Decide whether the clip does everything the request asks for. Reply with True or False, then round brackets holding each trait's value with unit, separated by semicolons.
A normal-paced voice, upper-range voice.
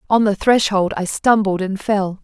True (190 wpm; 200 Hz)